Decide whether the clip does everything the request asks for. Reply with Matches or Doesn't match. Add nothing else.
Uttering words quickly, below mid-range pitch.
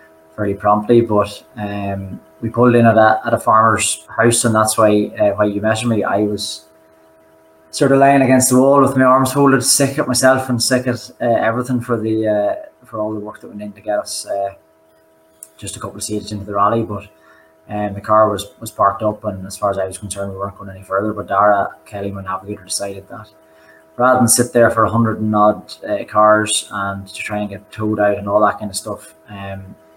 Matches